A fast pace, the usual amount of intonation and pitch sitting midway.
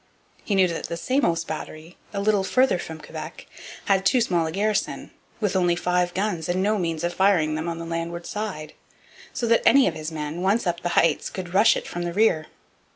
Yes: fast, 215 wpm; average, 3.3 semitones; medium, 175 Hz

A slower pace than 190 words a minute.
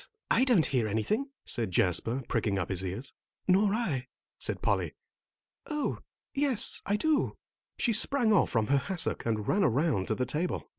Yes: average, 165 wpm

